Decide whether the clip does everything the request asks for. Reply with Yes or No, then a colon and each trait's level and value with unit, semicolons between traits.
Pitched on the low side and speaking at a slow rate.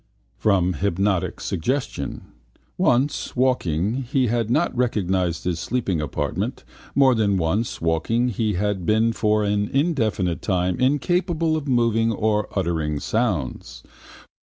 Yes: low, 105 Hz; slow, 120 wpm